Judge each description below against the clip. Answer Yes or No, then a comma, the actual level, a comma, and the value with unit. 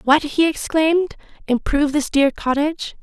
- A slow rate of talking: Yes, slow, 120 wpm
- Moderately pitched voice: No, very high, 295 Hz